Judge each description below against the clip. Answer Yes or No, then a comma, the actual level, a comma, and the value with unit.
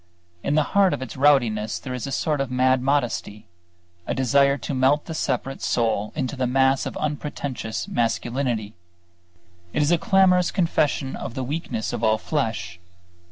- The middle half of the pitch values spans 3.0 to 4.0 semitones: Yes, average, 3.7 semitones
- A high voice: No, low, 135 Hz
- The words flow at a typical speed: Yes, average, 165 wpm